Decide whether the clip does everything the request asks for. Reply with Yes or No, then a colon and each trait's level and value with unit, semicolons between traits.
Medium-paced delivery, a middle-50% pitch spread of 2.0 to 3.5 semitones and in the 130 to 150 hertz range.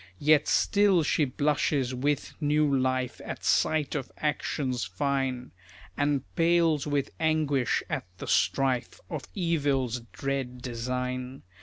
No: slow, 120 wpm; average, 2.8 semitones; medium, 140 Hz